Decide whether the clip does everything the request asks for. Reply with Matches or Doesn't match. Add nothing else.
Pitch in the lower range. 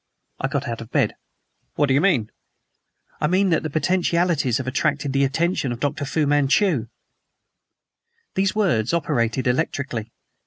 Doesn't match